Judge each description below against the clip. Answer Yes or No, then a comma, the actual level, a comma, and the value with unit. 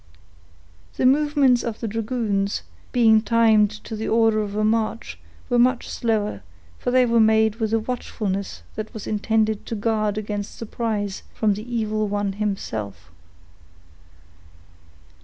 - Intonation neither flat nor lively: No, narrow, 1.8 semitones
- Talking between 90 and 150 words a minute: Yes, average, 140 wpm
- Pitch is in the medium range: No, high, 220 Hz